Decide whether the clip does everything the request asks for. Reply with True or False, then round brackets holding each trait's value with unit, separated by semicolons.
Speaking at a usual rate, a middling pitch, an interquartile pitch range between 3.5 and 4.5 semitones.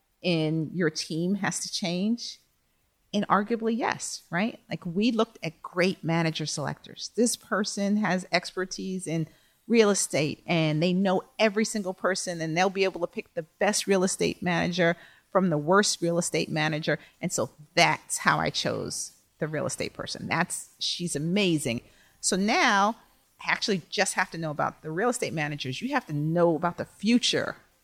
True (170 wpm; 180 Hz; 4.1 semitones)